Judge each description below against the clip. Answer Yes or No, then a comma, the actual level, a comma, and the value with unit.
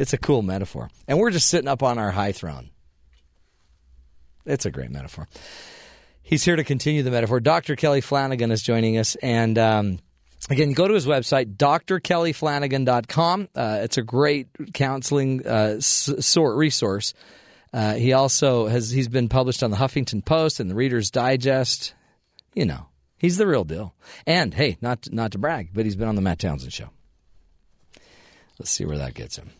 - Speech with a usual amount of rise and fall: No, wide, 6.7 semitones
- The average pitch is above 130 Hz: No, low, 125 Hz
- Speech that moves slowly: No, average, 175 wpm